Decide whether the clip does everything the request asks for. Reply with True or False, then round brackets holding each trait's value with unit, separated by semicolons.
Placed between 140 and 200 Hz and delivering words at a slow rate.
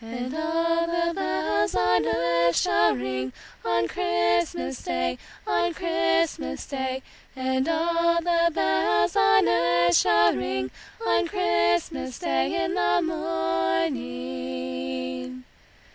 False (115 Hz; 105 wpm)